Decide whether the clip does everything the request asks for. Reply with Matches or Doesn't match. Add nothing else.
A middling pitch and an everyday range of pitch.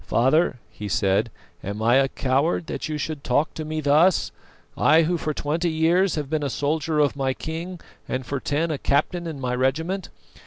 Matches